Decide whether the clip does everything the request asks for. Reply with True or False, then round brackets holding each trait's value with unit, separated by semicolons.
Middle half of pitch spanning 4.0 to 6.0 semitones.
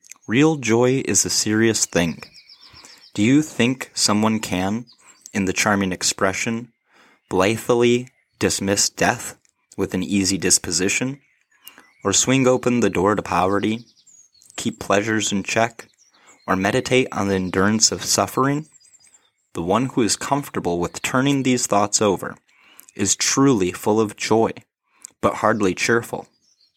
True (4.6 semitones)